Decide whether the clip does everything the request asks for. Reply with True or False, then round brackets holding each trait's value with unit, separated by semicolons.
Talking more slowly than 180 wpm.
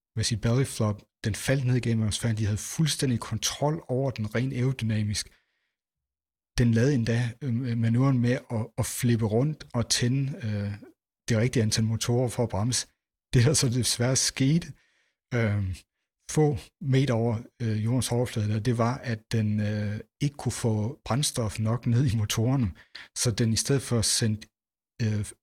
True (160 wpm)